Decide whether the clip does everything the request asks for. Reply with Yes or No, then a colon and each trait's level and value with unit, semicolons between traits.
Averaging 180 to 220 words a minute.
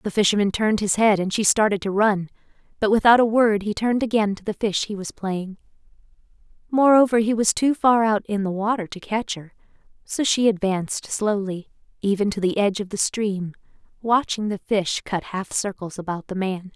Yes: average, 195 wpm